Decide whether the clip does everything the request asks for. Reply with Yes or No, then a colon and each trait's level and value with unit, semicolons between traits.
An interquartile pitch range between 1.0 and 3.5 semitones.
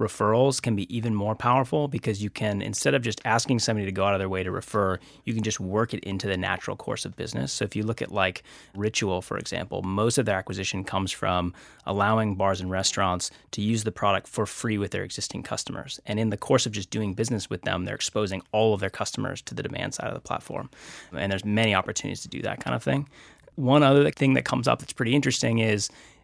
Yes: average, 3.2 semitones